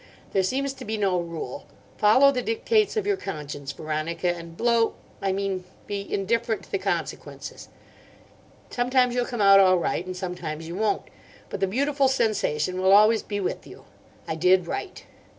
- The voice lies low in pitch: No, high, 195 Hz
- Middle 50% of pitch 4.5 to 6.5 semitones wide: Yes, average, 5.3 semitones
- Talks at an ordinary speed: Yes, average, 170 wpm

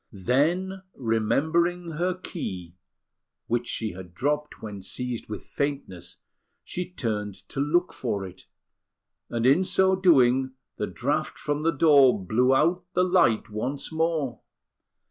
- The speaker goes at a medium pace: No, slow, 130 wpm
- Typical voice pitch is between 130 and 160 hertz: Yes, low, 135 Hz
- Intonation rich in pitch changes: Yes, wide, 7.2 semitones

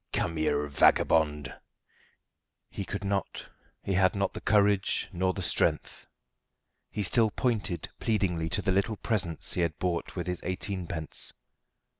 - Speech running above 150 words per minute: No, average, 140 wpm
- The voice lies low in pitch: Yes, very low, 95 Hz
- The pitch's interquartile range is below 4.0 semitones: Yes, average, 3.2 semitones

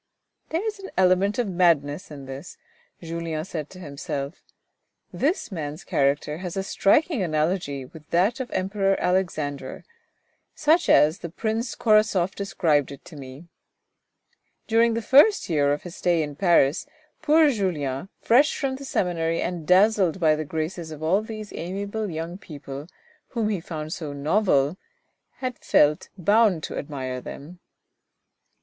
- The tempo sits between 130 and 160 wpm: Yes, average, 150 wpm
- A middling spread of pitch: No, wide, 5.7 semitones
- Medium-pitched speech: Yes, medium, 175 Hz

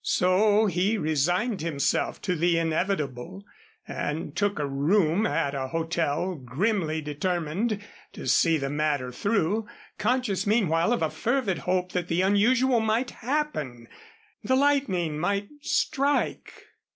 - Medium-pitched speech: Yes, medium, 180 Hz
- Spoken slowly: Yes, slow, 125 wpm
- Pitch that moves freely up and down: Yes, wide, 5.7 semitones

